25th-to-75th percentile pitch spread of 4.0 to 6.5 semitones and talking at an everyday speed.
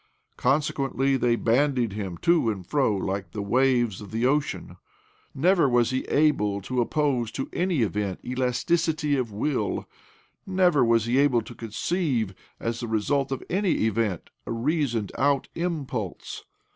Yes: average, 4.7 semitones; average, 150 wpm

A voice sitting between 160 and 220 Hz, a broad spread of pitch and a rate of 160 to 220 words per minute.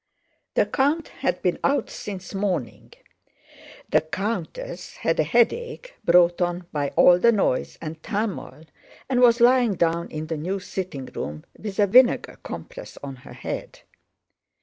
No: high, 190 Hz; wide, 6.4 semitones; average, 150 wpm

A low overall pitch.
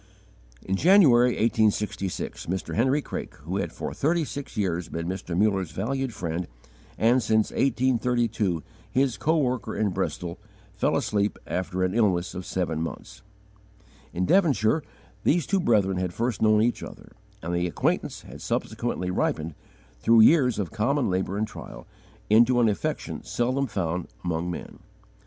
Yes: low, 105 Hz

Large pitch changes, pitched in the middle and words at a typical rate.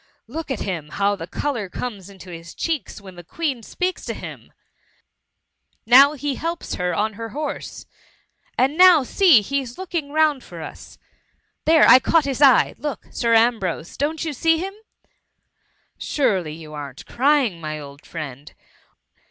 No: wide, 8.4 semitones; high, 245 Hz; average, 160 wpm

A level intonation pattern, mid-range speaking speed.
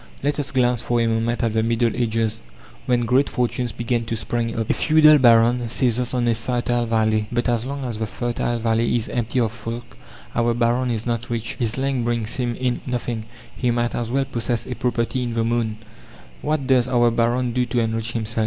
No: narrow, 1.4 semitones; fast, 210 wpm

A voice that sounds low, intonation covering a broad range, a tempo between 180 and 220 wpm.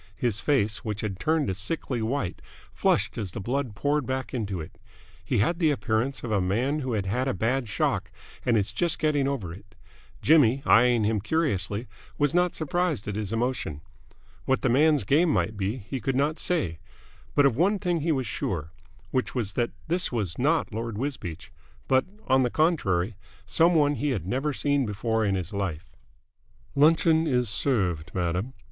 Yes: low, 125 Hz; wide, 6.0 semitones; average, 185 wpm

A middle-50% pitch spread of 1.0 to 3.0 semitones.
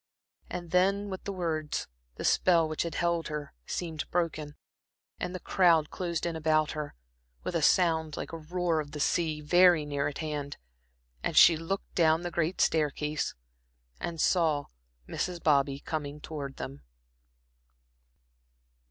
Yes: narrow, 2.5 semitones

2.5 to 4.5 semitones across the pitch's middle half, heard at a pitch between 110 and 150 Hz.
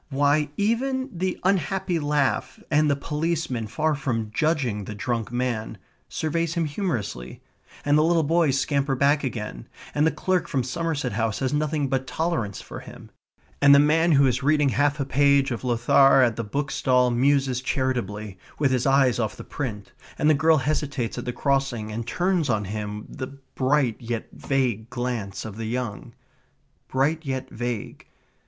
Yes: average, 4.0 semitones; low, 135 Hz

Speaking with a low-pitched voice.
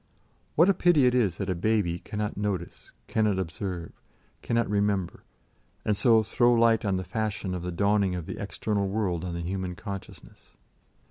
Yes: low, 100 Hz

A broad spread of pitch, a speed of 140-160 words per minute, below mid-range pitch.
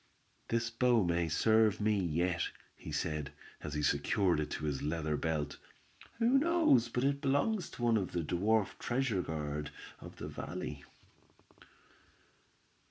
Yes: wide, 7.5 semitones; average, 145 wpm; very low, 95 Hz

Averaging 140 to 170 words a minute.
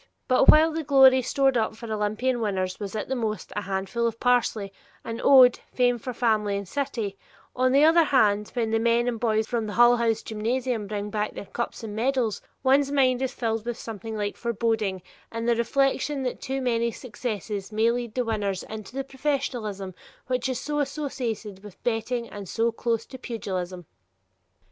No: average, 185 wpm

